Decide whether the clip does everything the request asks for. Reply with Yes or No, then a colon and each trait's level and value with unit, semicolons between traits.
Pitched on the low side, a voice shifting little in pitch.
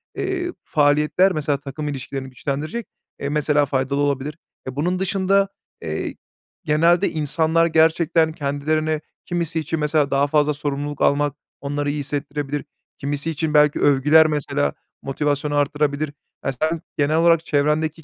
No: medium, 150 Hz; narrow, 2.0 semitones